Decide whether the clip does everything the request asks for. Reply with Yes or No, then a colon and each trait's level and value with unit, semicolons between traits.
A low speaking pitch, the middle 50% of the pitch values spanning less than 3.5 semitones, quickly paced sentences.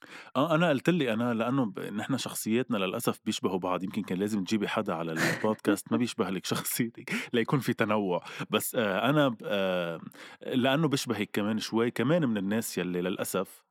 Yes: low, 110 Hz; average, 2.8 semitones; fast, 165 wpm